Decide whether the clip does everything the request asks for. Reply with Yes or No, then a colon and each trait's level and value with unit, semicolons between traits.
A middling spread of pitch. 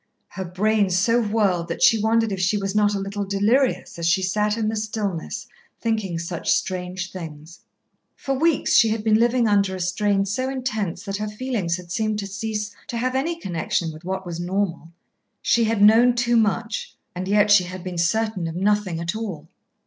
Yes: average, 3.4 semitones